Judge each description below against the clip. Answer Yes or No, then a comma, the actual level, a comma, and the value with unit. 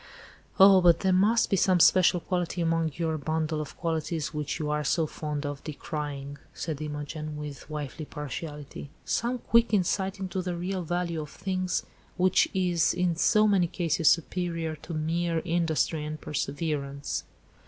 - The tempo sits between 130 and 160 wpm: Yes, average, 155 wpm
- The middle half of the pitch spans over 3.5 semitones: No, average, 3.2 semitones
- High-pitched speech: No, medium, 165 Hz